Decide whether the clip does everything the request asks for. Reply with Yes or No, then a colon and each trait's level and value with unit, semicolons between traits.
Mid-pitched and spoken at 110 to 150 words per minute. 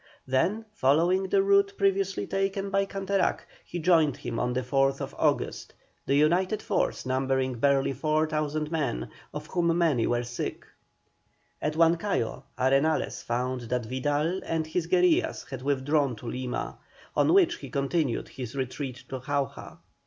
Yes: medium, 150 Hz; average, 145 wpm